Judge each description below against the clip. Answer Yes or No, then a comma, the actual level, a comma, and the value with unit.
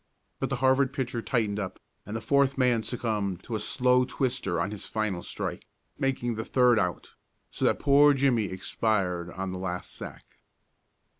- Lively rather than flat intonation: No, average, 4.9 semitones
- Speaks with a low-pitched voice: Yes, low, 115 Hz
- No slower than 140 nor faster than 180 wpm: Yes, average, 170 wpm